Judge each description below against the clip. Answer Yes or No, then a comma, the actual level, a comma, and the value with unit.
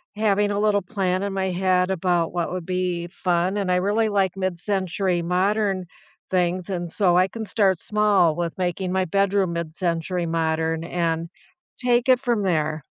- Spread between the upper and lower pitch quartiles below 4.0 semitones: Yes, narrow, 2.5 semitones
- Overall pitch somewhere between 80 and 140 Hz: No, medium, 185 Hz